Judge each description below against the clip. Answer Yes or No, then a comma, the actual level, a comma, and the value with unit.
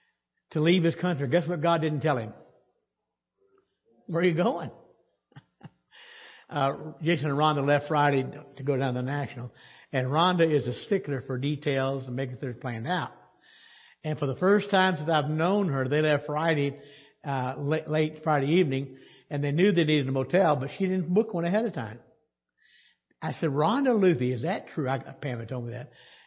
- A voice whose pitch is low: No, medium, 150 Hz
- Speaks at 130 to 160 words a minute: No, average, 190 wpm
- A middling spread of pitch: Yes, average, 4.4 semitones